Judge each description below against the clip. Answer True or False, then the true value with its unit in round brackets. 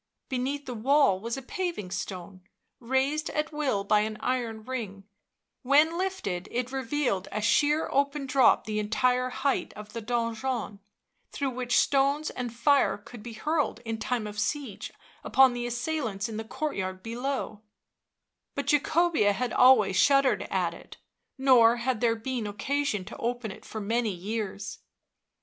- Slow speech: False (155 wpm)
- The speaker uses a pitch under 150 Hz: False (245 Hz)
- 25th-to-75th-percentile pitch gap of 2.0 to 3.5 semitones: False (4.4 semitones)